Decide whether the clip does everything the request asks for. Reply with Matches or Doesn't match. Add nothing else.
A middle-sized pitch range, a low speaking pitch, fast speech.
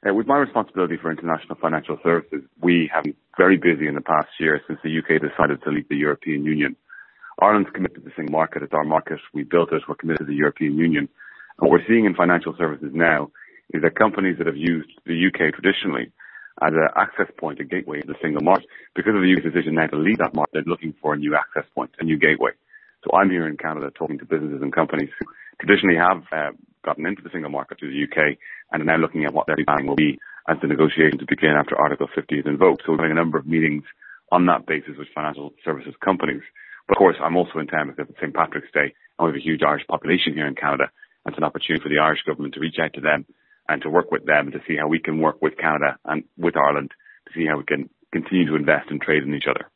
Doesn't match